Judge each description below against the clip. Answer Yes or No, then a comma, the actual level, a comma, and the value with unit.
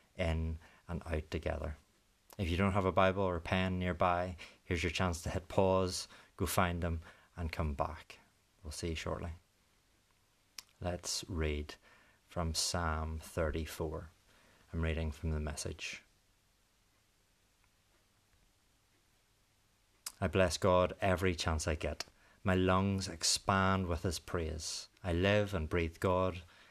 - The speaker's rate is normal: No, slow, 130 wpm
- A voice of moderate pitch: No, very low, 90 Hz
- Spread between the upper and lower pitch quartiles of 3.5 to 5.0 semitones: No, average, 3.1 semitones